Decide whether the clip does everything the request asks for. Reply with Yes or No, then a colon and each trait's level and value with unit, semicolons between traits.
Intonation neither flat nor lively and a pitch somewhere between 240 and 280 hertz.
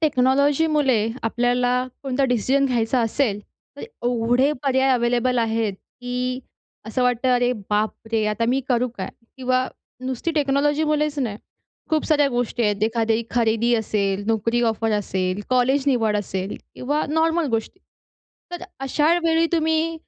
Yes: average, 3.7 semitones; very high, 250 Hz